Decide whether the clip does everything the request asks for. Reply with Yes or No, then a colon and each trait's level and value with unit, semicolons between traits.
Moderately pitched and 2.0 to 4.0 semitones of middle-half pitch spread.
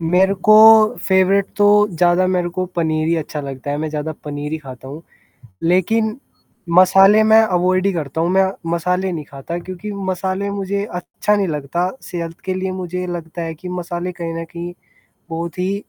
Yes: medium, 180 Hz; average, 2.7 semitones